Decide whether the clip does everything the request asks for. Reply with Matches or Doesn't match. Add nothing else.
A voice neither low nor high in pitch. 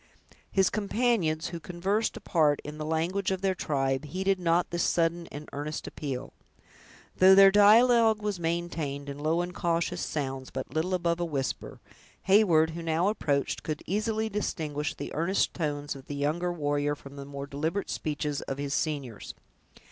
Matches